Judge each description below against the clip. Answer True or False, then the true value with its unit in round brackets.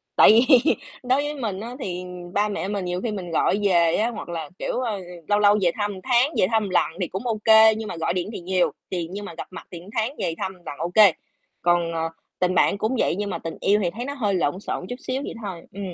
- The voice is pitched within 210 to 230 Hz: False (200 Hz)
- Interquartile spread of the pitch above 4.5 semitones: False (3.8 semitones)